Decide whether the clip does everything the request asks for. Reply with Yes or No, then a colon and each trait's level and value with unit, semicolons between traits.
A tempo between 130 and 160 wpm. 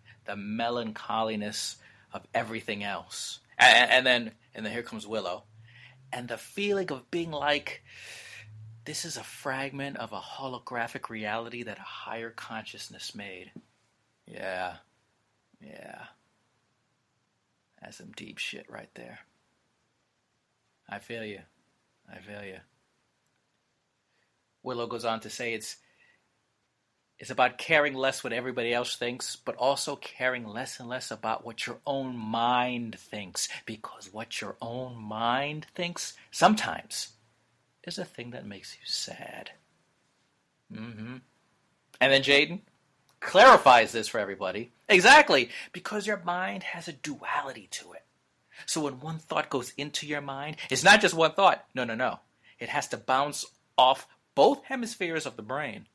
Yes: average, 140 wpm